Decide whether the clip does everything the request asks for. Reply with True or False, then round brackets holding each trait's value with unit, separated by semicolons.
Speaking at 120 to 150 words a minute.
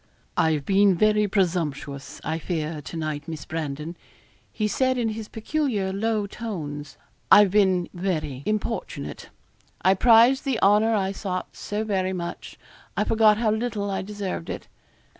True (145 wpm)